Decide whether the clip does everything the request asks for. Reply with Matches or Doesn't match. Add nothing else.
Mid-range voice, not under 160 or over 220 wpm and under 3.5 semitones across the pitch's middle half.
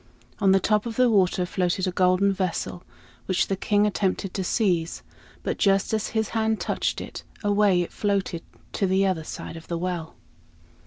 Doesn't match